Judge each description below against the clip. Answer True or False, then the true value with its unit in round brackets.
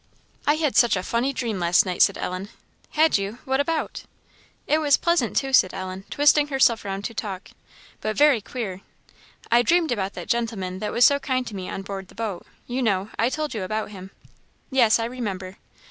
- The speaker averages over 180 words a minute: True (200 wpm)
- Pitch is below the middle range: False (230 Hz)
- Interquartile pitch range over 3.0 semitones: True (5.6 semitones)